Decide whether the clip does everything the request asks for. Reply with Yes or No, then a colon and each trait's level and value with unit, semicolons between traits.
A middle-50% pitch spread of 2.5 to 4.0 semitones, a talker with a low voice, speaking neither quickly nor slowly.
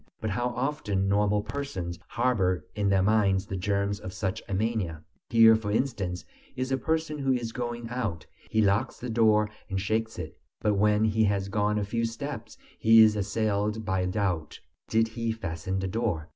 Yes: average, 2.8 semitones; low, 105 Hz; average, 185 wpm